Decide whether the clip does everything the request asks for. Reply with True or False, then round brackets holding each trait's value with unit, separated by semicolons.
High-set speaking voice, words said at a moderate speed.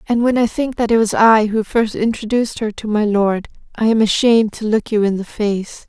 False (220 Hz; 245 wpm)